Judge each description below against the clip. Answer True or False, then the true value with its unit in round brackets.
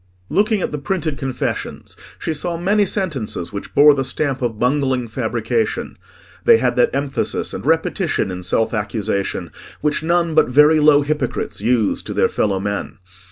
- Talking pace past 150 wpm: True (160 wpm)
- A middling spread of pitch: False (5.8 semitones)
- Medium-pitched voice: True (145 Hz)